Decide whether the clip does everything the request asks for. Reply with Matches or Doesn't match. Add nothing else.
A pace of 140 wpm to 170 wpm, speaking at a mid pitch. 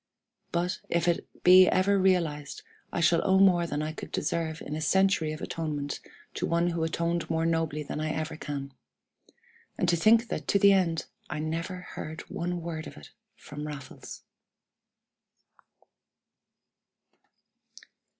Matches